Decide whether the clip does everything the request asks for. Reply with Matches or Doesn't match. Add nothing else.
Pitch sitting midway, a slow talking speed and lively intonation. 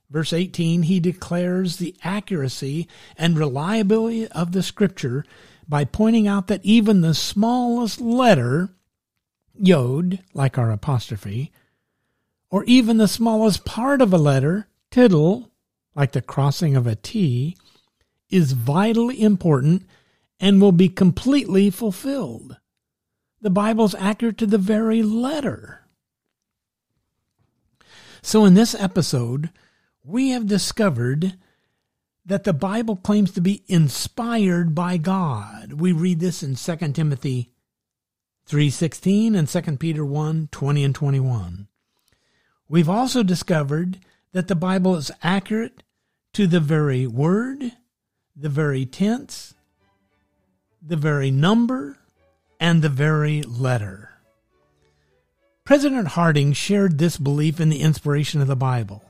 Matches